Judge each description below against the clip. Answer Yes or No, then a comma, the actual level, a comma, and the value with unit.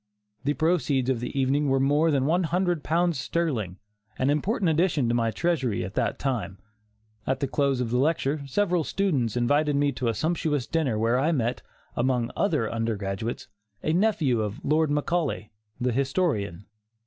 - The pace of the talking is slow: No, average, 170 wpm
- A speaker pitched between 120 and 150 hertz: Yes, medium, 140 Hz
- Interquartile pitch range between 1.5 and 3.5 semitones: No, average, 5.1 semitones